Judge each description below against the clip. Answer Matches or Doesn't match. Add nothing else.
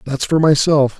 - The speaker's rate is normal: Matches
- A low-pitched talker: Doesn't match